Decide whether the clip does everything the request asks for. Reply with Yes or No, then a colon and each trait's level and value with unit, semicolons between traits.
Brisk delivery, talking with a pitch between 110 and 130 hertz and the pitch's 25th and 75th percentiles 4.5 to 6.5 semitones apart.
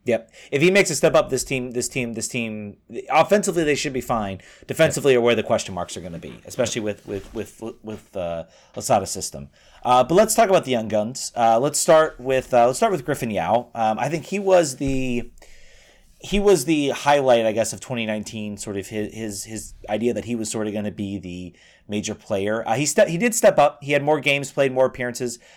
Yes: fast, 235 wpm; low, 120 Hz; average, 5.2 semitones